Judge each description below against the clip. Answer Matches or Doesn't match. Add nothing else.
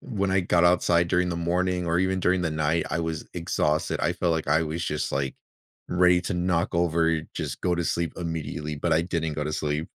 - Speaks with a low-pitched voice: Matches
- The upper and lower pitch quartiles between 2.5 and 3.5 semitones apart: Doesn't match